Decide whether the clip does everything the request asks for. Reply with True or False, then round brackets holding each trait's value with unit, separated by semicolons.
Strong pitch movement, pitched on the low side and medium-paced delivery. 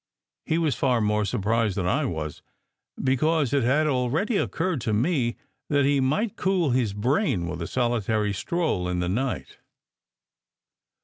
True (6.5 semitones; 125 Hz; 150 wpm)